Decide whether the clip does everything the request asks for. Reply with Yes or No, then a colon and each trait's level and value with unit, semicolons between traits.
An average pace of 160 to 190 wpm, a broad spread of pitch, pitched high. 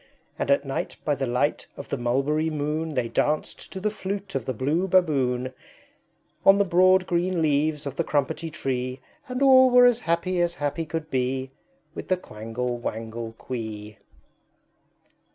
No: average, 165 wpm; wide, 5.7 semitones; medium, 150 Hz